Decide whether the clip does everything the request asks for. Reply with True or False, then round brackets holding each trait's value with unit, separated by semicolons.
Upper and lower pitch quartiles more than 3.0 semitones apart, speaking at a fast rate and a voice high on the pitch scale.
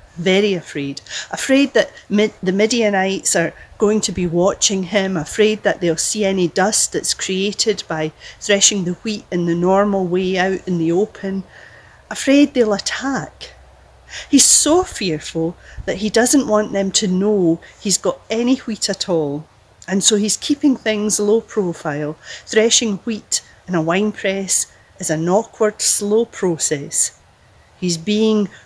False (3.5 semitones; 150 wpm; 200 Hz)